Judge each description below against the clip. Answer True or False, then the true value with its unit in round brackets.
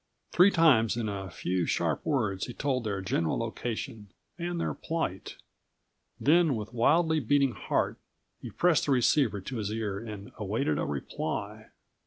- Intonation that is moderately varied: False (6.4 semitones)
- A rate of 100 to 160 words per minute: True (155 wpm)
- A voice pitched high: False (115 Hz)